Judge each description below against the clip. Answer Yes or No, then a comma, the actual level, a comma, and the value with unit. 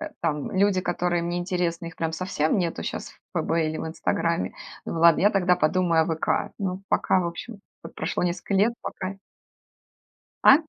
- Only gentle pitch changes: Yes, narrow, 2.1 semitones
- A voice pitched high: No, medium, 175 Hz